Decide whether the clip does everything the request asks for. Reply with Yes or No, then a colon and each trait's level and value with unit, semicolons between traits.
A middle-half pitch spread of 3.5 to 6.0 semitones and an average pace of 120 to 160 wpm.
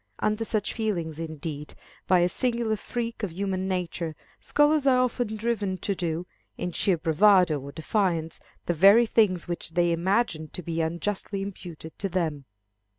Yes: average, 4.4 semitones; average, 155 wpm